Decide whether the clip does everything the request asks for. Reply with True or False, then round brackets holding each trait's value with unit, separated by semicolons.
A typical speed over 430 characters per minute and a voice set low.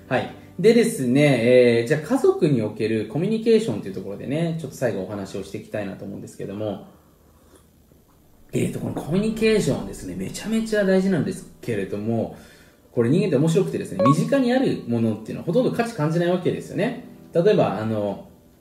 True (450 characters per minute; 125 Hz)